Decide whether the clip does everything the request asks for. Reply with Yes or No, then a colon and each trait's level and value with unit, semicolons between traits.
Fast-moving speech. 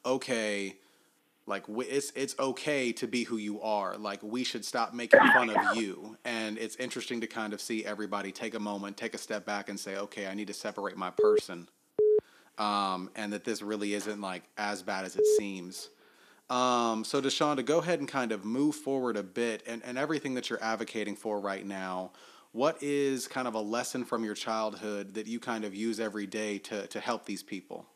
Yes: fast, 210 wpm